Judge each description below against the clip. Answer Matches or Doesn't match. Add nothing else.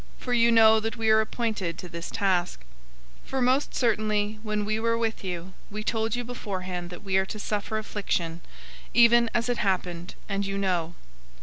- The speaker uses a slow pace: Doesn't match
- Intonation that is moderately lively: Matches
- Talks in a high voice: Matches